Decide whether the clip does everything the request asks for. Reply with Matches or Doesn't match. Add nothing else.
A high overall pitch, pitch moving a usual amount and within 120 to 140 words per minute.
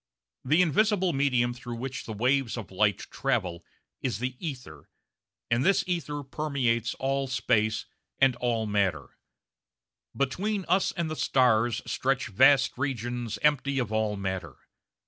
Doesn't match